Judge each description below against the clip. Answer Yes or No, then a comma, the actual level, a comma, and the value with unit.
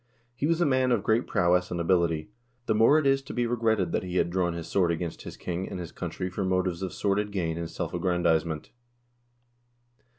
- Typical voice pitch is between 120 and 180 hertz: No, very low, 95 Hz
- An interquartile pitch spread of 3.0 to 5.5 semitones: Yes, average, 4.4 semitones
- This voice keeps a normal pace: No, fast, 210 wpm